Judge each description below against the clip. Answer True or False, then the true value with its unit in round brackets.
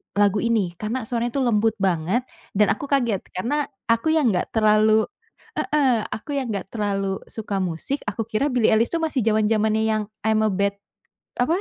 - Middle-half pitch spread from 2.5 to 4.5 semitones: True (2.9 semitones)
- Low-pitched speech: False (220 Hz)